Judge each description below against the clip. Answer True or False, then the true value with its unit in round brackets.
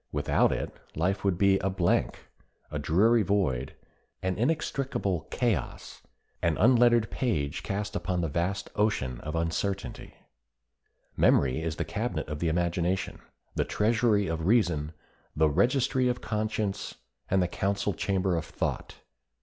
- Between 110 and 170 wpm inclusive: True (135 wpm)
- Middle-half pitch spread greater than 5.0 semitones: False (4.7 semitones)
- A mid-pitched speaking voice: False (95 Hz)